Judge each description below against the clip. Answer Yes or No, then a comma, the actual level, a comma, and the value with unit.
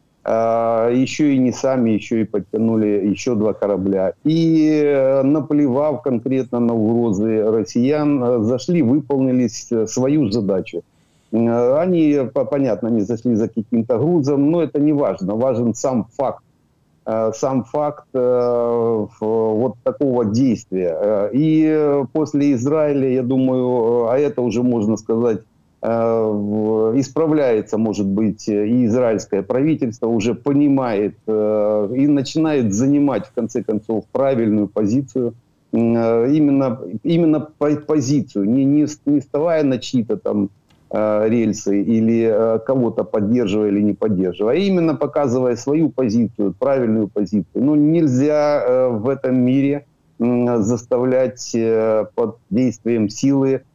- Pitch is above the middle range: No, low, 125 Hz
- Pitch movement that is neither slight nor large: Yes, average, 4.4 semitones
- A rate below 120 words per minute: Yes, average, 110 wpm